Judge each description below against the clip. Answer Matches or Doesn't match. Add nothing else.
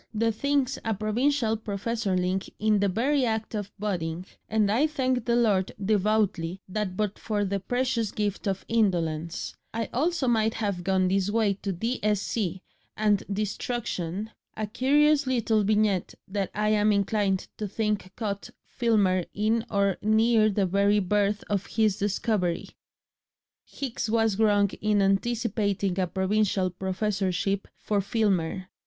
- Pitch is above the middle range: Matches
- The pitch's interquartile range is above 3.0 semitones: Doesn't match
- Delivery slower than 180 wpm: Matches